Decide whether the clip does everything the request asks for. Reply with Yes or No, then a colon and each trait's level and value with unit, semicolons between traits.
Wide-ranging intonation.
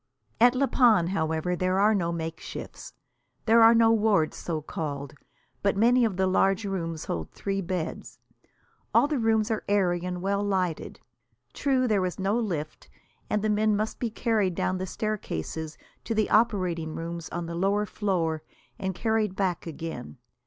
No: average, 4.3 semitones